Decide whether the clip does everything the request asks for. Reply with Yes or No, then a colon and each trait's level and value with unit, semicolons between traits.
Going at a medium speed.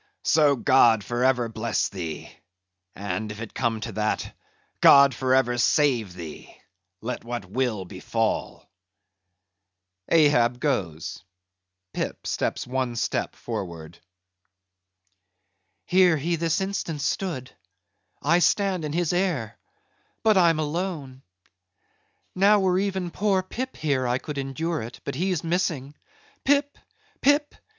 No: slow, 115 wpm